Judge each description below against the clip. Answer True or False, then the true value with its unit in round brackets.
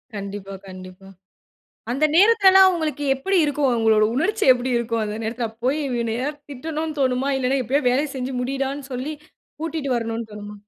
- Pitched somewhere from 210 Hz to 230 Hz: False (260 Hz)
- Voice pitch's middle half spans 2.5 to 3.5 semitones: False (4.7 semitones)